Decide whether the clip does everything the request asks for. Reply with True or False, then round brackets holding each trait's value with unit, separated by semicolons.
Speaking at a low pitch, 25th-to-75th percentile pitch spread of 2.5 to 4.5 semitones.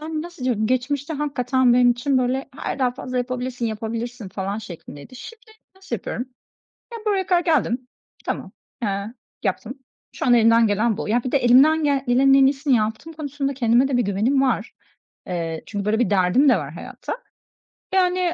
False (250 Hz; 4.0 semitones)